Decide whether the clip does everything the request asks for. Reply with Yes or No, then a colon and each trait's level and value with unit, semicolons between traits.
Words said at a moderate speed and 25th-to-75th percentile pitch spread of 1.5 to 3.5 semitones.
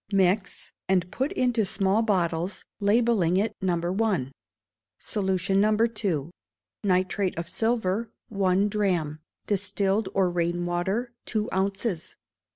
No: slow, 115 wpm; average, 2.8 semitones